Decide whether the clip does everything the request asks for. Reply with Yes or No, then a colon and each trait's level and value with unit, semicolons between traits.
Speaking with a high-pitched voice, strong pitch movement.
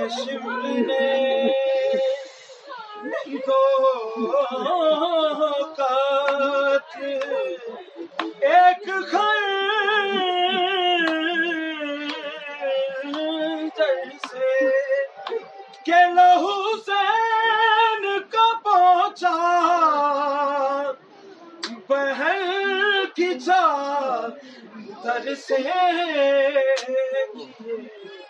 Yes: very high, 310 Hz; wide, 5.7 semitones